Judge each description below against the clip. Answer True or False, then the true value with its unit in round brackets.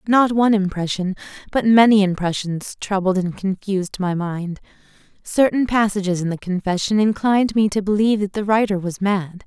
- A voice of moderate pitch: False (200 Hz)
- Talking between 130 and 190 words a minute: True (160 wpm)